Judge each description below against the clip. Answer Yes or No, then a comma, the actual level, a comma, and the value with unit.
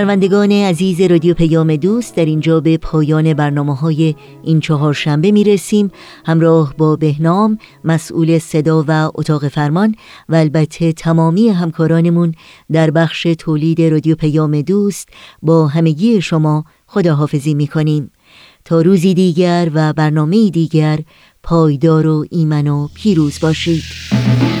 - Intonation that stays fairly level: Yes, narrow, 2.0 semitones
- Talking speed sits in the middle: Yes, average, 125 wpm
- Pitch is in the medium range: Yes, medium, 160 Hz